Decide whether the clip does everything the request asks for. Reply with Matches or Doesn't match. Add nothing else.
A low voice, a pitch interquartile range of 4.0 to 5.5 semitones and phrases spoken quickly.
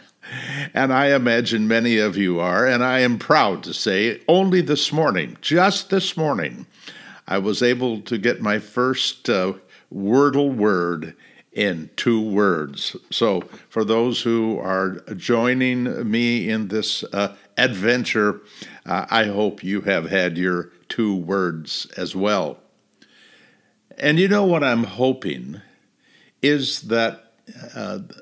Doesn't match